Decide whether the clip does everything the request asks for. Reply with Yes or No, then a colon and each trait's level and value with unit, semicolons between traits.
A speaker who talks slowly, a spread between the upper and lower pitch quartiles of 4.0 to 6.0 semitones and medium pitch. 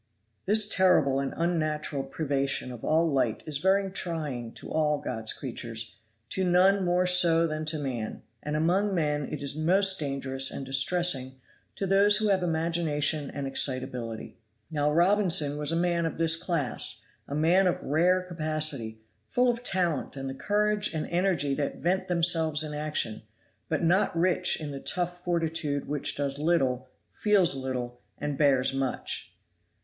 No: average, 160 wpm; average, 4.4 semitones; medium, 155 Hz